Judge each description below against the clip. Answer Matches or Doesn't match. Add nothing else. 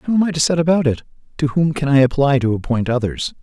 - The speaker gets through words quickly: Matches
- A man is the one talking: Matches